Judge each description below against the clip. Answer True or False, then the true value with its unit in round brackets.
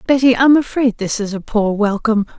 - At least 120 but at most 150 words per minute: False (200 wpm)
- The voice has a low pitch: False (230 Hz)